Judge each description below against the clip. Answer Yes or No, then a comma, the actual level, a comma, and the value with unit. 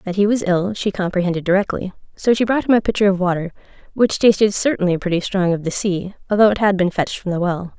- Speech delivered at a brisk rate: Yes, fast, 240 wpm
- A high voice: Yes, high, 195 Hz